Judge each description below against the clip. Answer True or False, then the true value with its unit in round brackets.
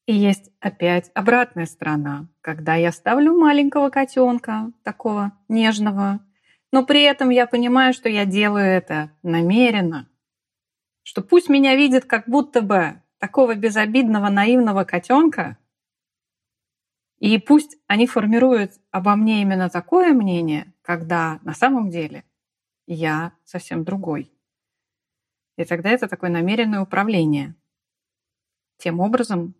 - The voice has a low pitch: False (205 Hz)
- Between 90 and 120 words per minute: True (115 wpm)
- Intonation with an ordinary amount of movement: False (6.3 semitones)